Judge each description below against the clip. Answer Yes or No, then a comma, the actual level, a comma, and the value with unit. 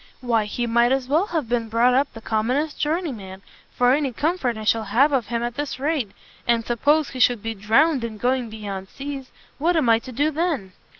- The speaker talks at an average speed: No, fast, 215 wpm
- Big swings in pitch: No, average, 4.3 semitones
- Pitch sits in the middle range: No, high, 245 Hz